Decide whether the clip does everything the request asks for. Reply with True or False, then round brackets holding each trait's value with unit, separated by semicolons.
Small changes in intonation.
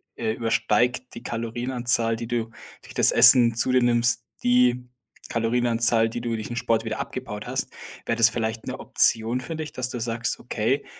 True (1.4 semitones)